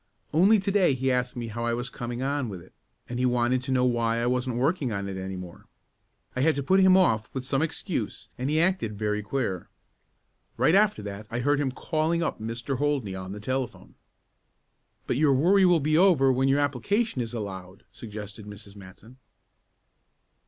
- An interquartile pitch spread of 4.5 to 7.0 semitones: Yes, average, 5.1 semitones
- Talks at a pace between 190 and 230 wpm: Yes, average, 195 wpm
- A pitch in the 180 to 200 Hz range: No, low, 125 Hz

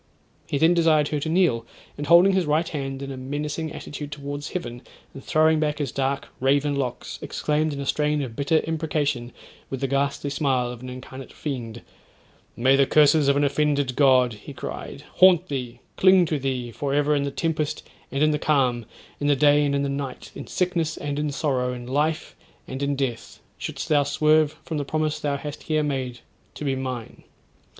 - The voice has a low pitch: No, medium, 145 Hz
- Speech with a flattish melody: Yes, narrow, 2.3 semitones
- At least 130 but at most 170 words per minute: No, average, 200 wpm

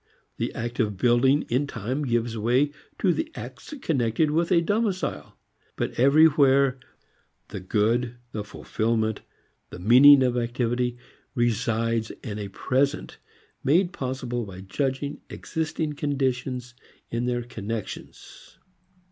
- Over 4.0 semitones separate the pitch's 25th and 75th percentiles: No, average, 3.7 semitones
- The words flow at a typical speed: No, slow, 120 wpm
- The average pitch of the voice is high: No, low, 125 Hz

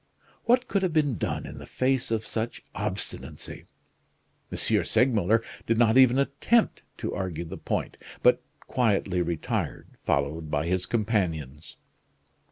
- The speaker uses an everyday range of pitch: No, wide, 6.8 semitones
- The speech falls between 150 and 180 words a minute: No, slow, 135 wpm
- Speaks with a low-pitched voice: Yes, low, 110 Hz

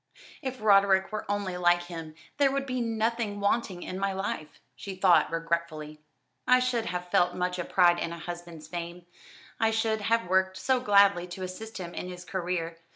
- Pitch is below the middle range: No, medium, 185 Hz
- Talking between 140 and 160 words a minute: No, average, 185 wpm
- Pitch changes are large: No, average, 3.8 semitones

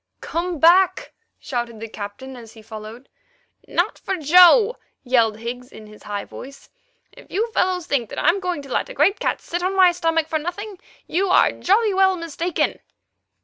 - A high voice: Yes, very high, 325 Hz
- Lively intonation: Yes, wide, 7.3 semitones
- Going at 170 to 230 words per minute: Yes, average, 180 wpm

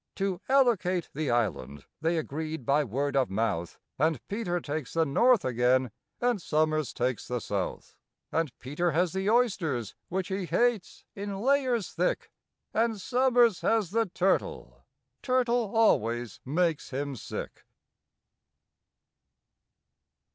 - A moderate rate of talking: No, slow, 120 wpm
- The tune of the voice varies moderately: No, wide, 8.5 semitones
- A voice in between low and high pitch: Yes, medium, 170 Hz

